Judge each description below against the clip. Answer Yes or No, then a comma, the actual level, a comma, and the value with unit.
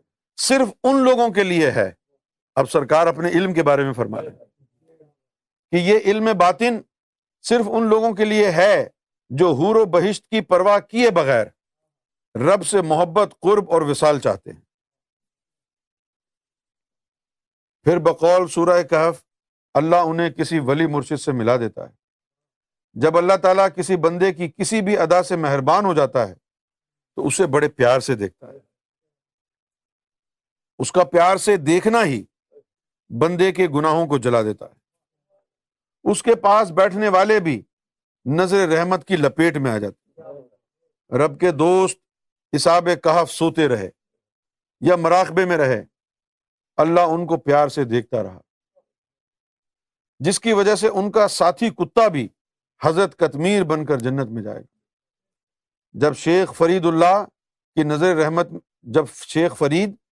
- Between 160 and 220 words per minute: No, average, 145 wpm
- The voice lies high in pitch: No, medium, 175 Hz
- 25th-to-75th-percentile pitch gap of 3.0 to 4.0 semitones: No, average, 4.4 semitones